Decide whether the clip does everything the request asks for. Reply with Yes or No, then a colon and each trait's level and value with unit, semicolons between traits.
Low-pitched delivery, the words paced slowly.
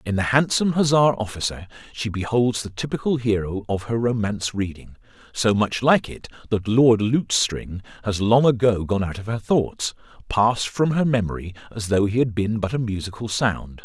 No: low, 110 Hz; average, 180 wpm